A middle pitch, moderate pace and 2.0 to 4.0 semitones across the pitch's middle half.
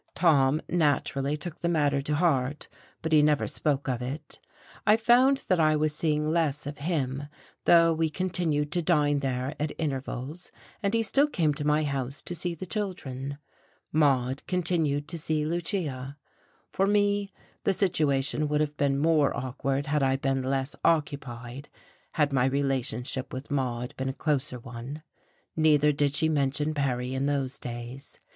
Yes: medium, 145 Hz; average, 165 wpm; average, 3.1 semitones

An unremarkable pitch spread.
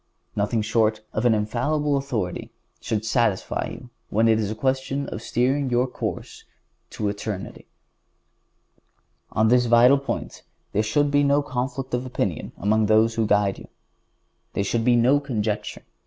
Yes: average, 3.4 semitones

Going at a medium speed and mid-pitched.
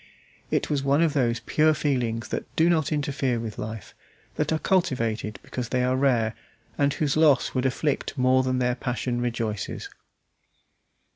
No: average, 160 wpm; low, 130 Hz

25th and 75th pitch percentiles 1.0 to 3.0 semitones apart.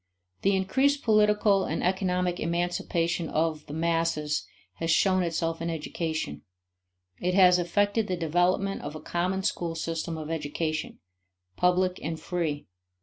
Yes: narrow, 2.5 semitones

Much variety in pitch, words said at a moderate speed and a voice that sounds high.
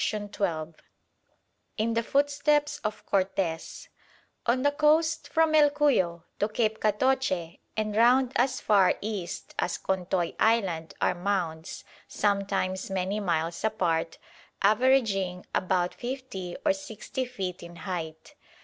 No: wide, 6.2 semitones; slow, 120 wpm; high, 205 Hz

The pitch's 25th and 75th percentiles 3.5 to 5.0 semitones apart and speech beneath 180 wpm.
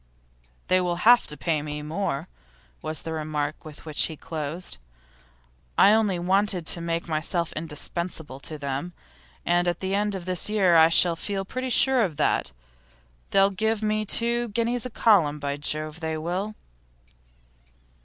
Yes: average, 4.7 semitones; average, 165 wpm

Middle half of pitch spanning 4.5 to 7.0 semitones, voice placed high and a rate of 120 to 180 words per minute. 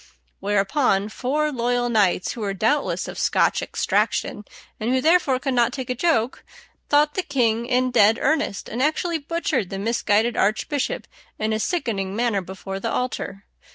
Yes: average, 5.2 semitones; high, 240 Hz; average, 160 wpm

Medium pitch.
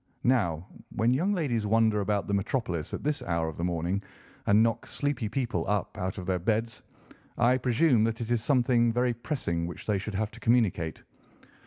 No: low, 110 Hz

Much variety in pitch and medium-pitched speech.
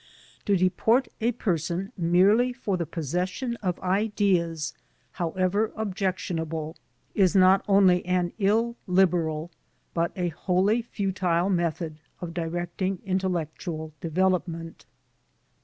No: average, 2.7 semitones; medium, 180 Hz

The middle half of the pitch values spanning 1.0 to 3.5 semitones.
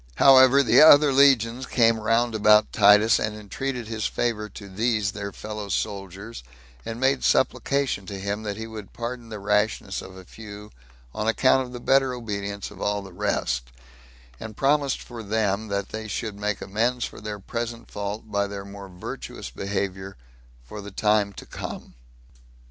Yes: average, 2.7 semitones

